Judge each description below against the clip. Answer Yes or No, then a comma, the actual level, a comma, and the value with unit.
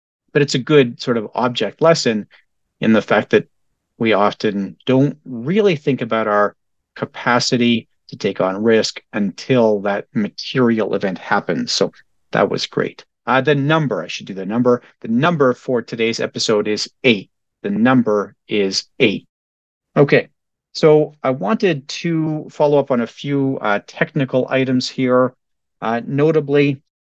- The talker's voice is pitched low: Yes, low, 125 Hz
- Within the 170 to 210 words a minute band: No, average, 150 wpm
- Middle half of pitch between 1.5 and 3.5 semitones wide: No, average, 5.1 semitones